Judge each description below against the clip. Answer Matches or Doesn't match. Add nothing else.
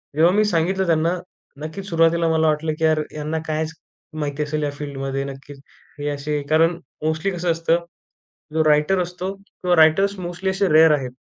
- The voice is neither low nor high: Matches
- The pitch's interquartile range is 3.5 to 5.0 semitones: Doesn't match